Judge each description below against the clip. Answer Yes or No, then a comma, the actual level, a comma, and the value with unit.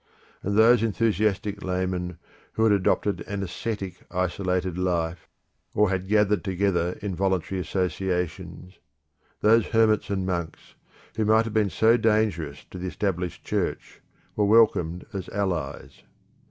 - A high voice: No, very low, 95 Hz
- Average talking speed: No, slow, 130 wpm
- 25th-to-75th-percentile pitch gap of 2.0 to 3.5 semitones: Yes, average, 2.8 semitones